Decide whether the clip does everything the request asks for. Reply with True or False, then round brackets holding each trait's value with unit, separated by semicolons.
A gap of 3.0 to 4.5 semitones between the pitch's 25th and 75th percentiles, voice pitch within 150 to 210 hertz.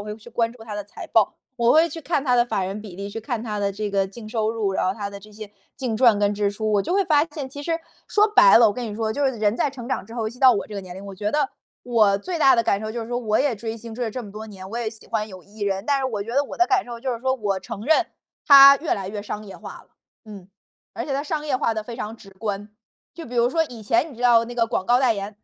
False (3.7 semitones; 225 Hz)